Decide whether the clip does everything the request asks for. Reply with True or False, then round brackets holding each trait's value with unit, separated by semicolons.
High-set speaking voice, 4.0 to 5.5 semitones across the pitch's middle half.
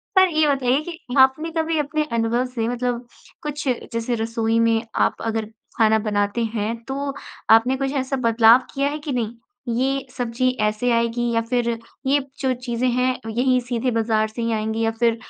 False (240 Hz; 2.8 semitones)